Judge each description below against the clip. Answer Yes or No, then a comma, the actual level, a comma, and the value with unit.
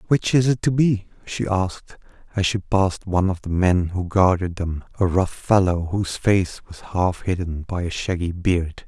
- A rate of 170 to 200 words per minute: Yes, average, 195 wpm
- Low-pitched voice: Yes, very low, 95 Hz